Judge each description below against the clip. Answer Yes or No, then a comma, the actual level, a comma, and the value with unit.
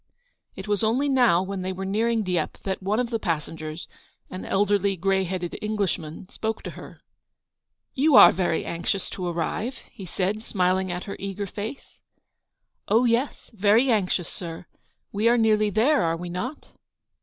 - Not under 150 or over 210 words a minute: Yes, average, 165 wpm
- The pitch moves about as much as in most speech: Yes, average, 3.5 semitones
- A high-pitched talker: Yes, high, 200 Hz